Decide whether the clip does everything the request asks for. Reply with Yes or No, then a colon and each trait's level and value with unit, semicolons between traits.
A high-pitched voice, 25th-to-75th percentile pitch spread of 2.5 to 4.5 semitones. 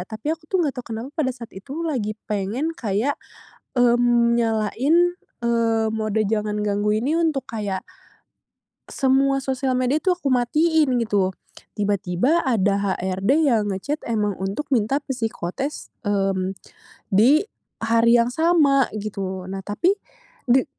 No: high, 235 Hz; average, 5.0 semitones